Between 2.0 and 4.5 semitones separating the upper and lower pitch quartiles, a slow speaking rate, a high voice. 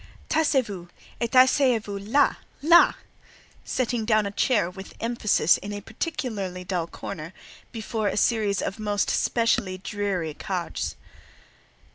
Yes: average, 3.7 semitones; slow, 120 wpm; high, 210 Hz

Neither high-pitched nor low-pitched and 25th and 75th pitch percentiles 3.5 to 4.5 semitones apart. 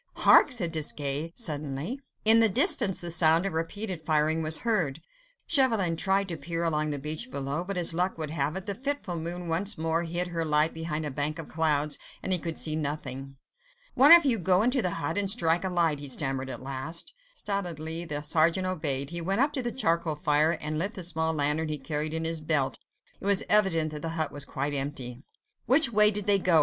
Yes: medium, 165 Hz; average, 4.0 semitones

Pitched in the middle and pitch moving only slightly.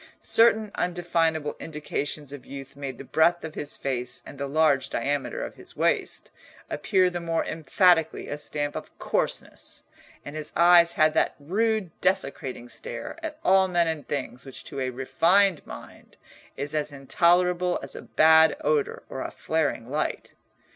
No: medium, 155 Hz; average, 3.7 semitones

